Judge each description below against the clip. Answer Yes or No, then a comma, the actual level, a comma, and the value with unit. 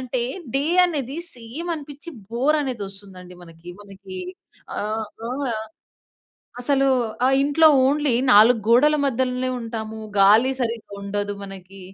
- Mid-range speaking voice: No, high, 235 Hz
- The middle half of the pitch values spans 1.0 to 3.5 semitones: No, average, 5.2 semitones